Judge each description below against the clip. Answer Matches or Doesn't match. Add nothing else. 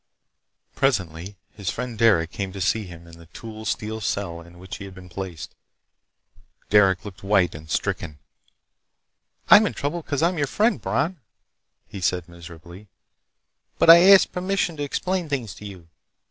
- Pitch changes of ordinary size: Doesn't match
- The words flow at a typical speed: Matches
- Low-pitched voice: Matches